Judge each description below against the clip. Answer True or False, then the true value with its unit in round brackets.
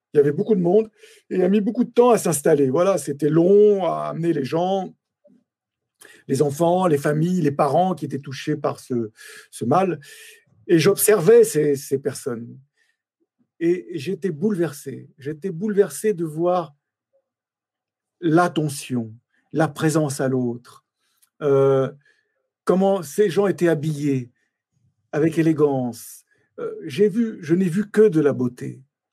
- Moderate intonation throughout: False (6.4 semitones)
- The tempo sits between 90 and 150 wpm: True (145 wpm)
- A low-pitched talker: False (165 Hz)